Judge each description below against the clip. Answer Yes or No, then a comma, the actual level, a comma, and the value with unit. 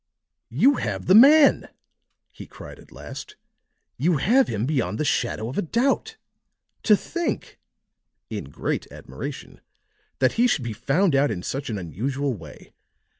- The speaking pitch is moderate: Yes, medium, 145 Hz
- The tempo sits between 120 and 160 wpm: Yes, average, 150 wpm